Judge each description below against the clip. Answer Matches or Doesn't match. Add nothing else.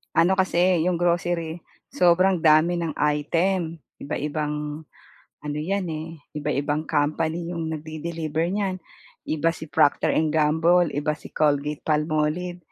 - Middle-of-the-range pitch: Matches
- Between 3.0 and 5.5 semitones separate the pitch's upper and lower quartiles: Doesn't match